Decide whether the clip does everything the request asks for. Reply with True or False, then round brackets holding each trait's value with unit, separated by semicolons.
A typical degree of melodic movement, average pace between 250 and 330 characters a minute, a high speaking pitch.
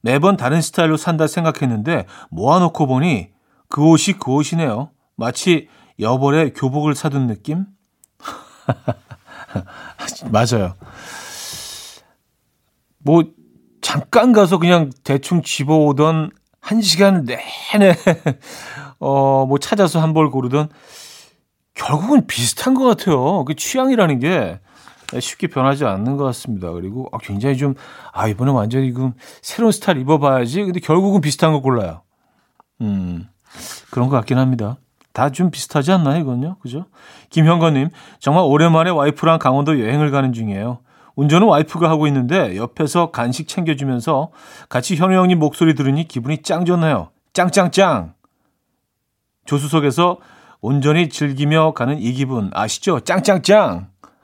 False (4.9 semitones; 280 characters per minute; 150 Hz)